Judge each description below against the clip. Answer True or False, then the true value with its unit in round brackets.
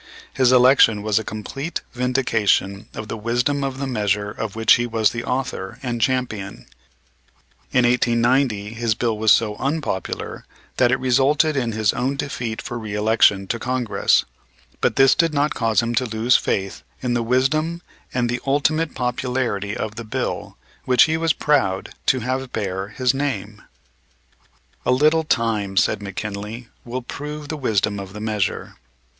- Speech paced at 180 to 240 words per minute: False (160 wpm)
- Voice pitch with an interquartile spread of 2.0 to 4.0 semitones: True (3.6 semitones)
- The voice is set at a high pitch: False (120 Hz)